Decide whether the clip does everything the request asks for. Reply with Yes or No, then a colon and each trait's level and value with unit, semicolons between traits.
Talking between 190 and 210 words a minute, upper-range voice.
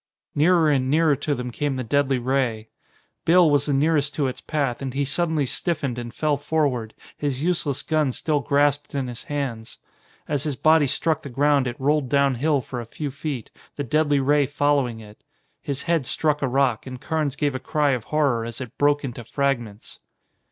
No: average, 195 wpm; medium, 140 Hz